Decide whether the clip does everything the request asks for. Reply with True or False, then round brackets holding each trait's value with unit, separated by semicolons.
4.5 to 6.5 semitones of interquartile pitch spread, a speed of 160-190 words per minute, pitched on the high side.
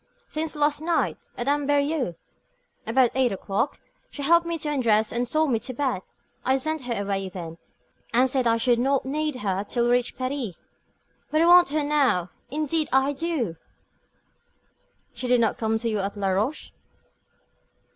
True (4.8 semitones; 165 wpm; 255 Hz)